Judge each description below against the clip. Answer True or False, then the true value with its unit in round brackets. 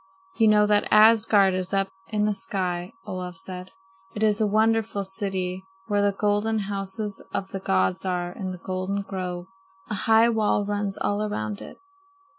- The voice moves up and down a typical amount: False (2.1 semitones)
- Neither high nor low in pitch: False (200 Hz)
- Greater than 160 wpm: True (170 wpm)